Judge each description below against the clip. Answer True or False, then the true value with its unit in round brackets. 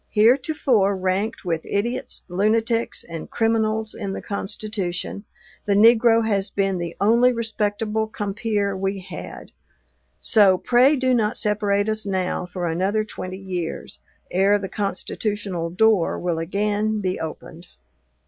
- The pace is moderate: False (130 wpm)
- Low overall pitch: False (205 Hz)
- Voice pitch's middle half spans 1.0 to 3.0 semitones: True (2.6 semitones)